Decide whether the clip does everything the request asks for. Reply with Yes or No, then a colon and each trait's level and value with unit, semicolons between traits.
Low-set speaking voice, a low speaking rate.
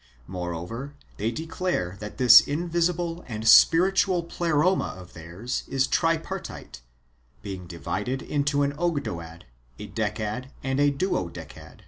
Yes: low, 130 Hz; slow, 115 wpm